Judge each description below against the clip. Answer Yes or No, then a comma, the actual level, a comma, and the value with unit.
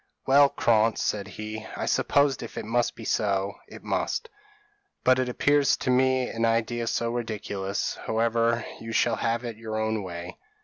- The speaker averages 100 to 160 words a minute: No, average, 170 wpm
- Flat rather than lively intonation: Yes, narrow, 2.0 semitones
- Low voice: Yes, low, 115 Hz